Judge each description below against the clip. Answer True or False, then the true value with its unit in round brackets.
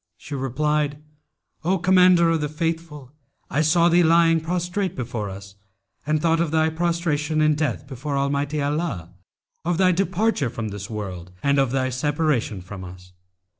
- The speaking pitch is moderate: True (150 Hz)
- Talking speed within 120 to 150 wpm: False (160 wpm)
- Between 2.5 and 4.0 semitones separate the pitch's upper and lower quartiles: False (4.4 semitones)